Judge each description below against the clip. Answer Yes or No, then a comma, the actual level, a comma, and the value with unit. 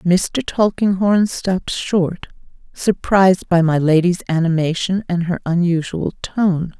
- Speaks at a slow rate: Yes, slow, 115 wpm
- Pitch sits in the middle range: Yes, medium, 180 Hz